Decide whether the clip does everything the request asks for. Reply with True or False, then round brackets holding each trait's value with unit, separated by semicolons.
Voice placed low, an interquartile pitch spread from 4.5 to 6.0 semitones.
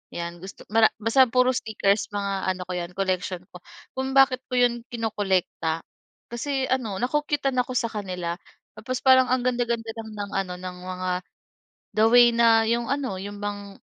False (225 Hz; 4.8 semitones)